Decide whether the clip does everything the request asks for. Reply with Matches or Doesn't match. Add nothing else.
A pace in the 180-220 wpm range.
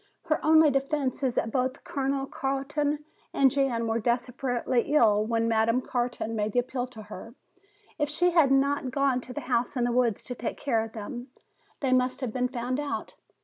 Matches